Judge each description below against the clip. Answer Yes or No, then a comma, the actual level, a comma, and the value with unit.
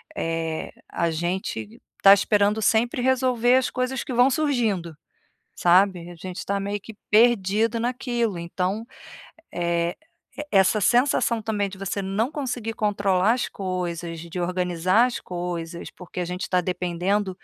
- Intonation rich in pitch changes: No, average, 4.5 semitones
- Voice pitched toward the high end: Yes, high, 195 Hz